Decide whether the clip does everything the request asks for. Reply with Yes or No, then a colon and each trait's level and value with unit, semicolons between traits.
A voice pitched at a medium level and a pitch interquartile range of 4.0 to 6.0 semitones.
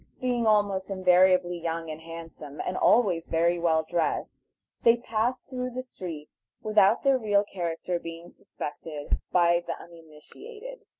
Yes: medium, 180 Hz; average, 4.8 semitones